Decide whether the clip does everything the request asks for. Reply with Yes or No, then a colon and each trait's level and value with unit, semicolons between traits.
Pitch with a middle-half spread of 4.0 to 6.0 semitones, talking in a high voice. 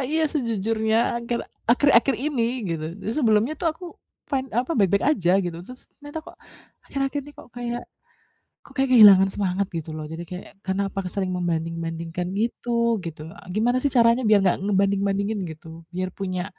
Yes: average, 4.8 semitones; high, 205 Hz